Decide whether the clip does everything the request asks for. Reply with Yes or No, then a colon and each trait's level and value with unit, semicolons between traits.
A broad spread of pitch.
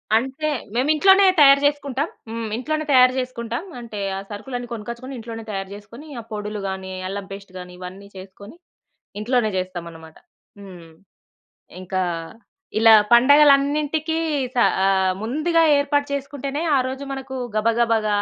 Yes: wide, 5.7 semitones